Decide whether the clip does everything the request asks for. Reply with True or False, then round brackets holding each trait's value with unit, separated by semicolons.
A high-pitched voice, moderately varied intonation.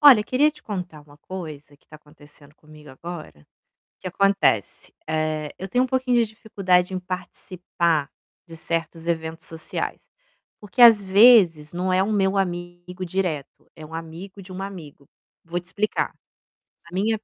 False (180 Hz; 3.8 semitones)